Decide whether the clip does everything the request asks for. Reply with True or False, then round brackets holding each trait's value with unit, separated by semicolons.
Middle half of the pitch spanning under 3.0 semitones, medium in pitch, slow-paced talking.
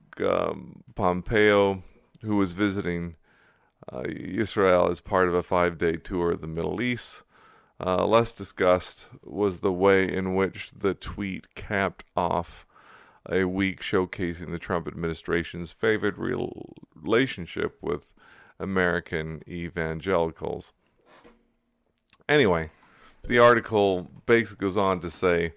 False (2.5 semitones; 90 Hz; 115 wpm)